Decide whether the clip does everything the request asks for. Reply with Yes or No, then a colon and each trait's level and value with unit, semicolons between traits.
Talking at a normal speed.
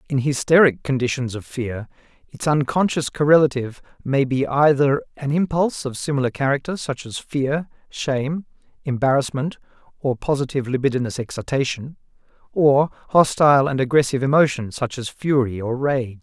No: slow, 130 wpm